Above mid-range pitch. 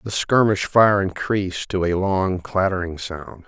No: very low, 95 Hz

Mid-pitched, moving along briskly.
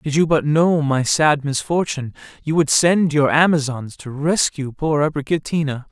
No: medium, 150 Hz; average, 160 wpm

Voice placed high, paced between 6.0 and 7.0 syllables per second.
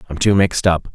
No: very low, 90 Hz; 6.8 syllables/s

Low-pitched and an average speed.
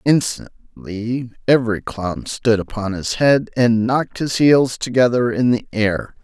Yes: low, 120 Hz; average, 145 wpm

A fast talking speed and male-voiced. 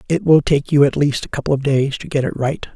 Yes: fast, 305 wpm; male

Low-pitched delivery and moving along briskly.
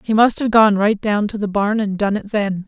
No: high, 210 Hz; fast, 290 wpm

